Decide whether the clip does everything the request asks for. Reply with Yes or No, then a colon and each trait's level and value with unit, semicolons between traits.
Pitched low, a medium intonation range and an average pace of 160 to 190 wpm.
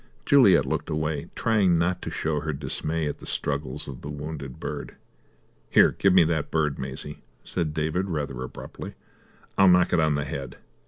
Yes: very low, 75 Hz; average, 3.1 semitones; average, 175 wpm